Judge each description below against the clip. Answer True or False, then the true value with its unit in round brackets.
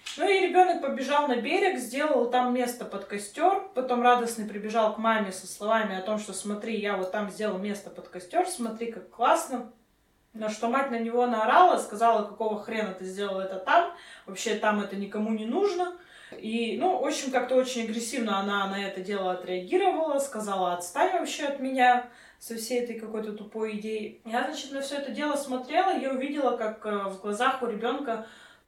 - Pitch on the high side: True (230 Hz)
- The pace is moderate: False (185 wpm)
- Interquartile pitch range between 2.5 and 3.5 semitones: False (4.4 semitones)